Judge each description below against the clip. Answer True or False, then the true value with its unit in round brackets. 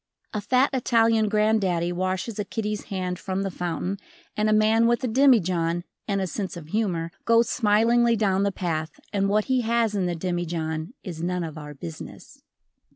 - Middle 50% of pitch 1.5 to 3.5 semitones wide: False (4.1 semitones)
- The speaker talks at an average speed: True (180 wpm)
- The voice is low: False (195 Hz)